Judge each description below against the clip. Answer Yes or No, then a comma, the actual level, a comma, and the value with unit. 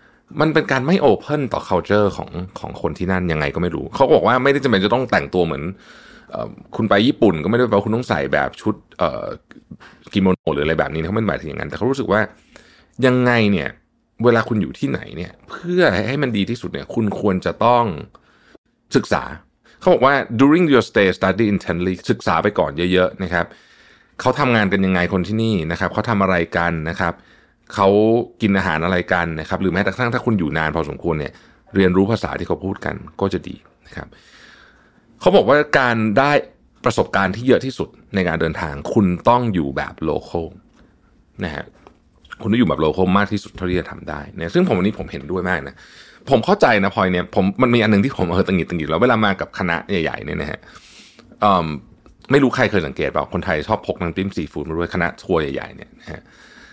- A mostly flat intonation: No, average, 4.6 semitones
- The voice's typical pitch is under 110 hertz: Yes, very low, 95 Hz